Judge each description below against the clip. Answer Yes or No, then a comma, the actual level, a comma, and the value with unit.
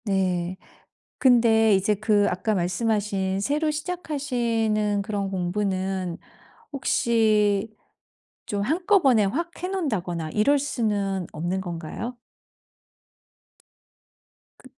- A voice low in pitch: No, high, 210 Hz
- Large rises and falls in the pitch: No, average, 4.4 semitones